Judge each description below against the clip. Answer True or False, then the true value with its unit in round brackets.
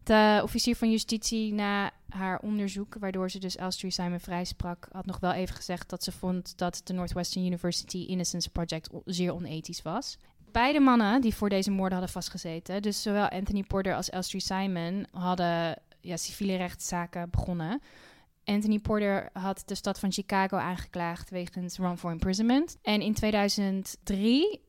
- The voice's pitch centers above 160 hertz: True (190 Hz)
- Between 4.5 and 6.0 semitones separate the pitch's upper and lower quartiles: False (2.5 semitones)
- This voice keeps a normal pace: True (160 wpm)